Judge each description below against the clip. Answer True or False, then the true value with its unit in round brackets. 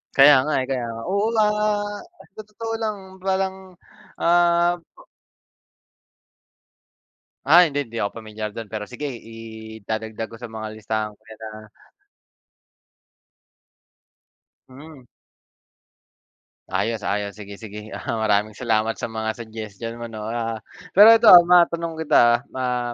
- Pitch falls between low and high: False (115 Hz)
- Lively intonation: True (7.5 semitones)